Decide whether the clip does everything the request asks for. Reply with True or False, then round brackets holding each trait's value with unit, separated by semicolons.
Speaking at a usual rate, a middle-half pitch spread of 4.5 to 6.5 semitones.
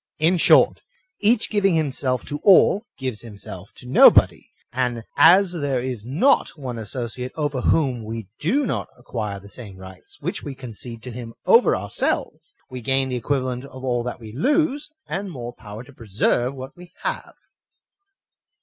True (165 wpm; 5.1 semitones)